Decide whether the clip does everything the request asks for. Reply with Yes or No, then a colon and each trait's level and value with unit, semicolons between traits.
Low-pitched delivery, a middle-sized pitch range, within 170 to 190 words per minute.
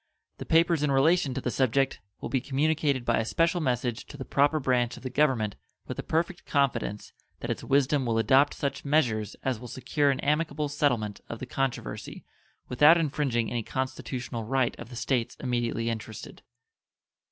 Yes: low, 130 Hz; average, 3.5 semitones; average, 175 wpm